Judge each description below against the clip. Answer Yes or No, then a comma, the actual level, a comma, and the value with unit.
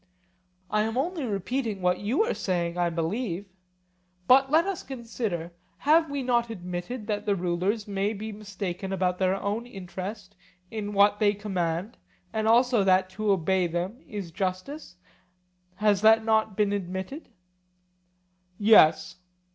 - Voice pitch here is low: No, high, 205 Hz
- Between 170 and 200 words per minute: No, average, 140 wpm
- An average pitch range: Yes, average, 3.5 semitones